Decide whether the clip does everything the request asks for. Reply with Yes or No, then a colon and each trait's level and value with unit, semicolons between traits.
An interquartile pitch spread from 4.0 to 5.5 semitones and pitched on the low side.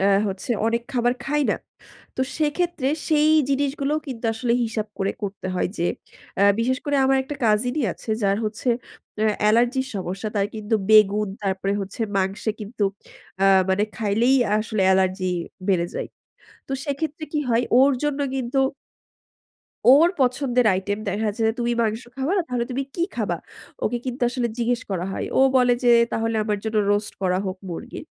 No: average, 4.5 semitones; high, 230 Hz